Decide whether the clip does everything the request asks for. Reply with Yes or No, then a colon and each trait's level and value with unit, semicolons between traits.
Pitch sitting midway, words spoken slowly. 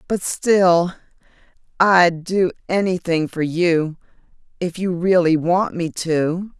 Yes: medium, 175 Hz; slow, 100 wpm